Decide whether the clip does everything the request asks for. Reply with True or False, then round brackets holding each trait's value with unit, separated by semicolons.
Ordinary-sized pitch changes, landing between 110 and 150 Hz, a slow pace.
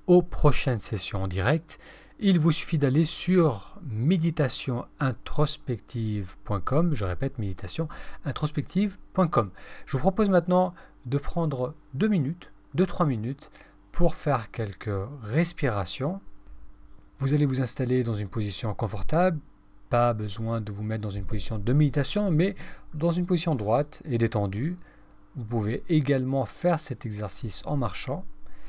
False (7.1 semitones; 135 Hz; 130 wpm)